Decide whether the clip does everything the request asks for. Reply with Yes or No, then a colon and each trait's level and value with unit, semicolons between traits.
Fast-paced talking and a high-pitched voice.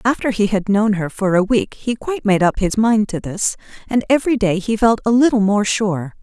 Yes: fast, 240 wpm; high, 210 Hz